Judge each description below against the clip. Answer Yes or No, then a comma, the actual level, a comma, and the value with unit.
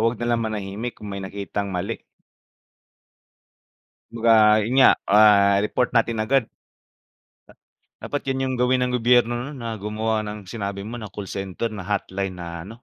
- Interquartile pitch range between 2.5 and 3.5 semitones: Yes, average, 3.0 semitones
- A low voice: Yes, low, 110 Hz